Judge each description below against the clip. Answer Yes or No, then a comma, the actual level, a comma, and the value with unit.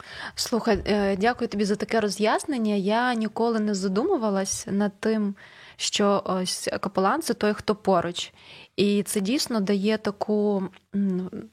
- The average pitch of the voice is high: Yes, high, 210 Hz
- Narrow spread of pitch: Yes, narrow, 1.8 semitones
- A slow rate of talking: No, average, 120 wpm